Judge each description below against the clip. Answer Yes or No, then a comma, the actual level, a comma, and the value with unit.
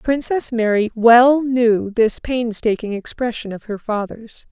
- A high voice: Yes, high, 230 Hz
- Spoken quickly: No, slow, 135 wpm